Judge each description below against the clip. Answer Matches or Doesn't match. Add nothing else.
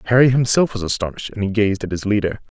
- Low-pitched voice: Matches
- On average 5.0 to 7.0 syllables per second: Doesn't match